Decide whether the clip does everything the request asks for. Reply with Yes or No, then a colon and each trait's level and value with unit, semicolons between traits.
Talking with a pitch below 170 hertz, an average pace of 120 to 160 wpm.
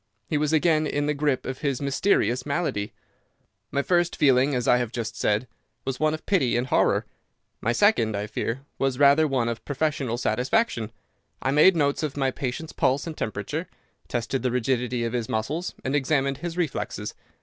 No: low, 135 Hz; average, 180 wpm